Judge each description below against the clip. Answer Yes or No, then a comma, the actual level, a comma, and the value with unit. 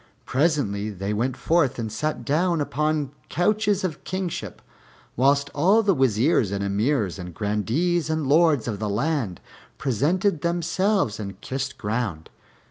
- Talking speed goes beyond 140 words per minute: No, slow, 135 wpm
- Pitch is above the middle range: No, medium, 140 Hz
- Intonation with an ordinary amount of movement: No, wide, 7.8 semitones